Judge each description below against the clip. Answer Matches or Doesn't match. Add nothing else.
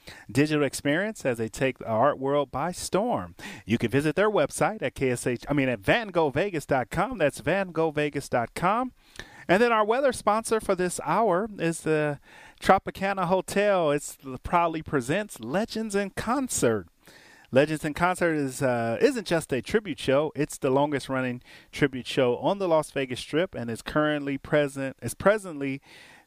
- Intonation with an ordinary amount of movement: Doesn't match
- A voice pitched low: Doesn't match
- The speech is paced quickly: Doesn't match